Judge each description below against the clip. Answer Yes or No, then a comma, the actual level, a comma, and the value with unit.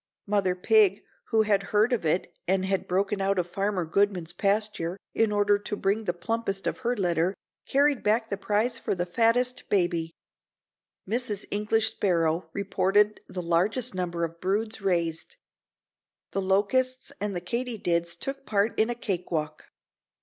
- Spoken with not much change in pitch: No, average, 3.7 semitones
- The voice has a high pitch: Yes, high, 200 Hz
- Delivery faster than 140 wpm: Yes, average, 155 wpm